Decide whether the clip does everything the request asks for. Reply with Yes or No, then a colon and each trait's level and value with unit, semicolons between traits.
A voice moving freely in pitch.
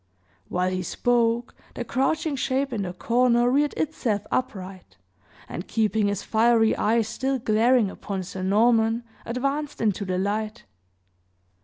No: average, 3.8 semitones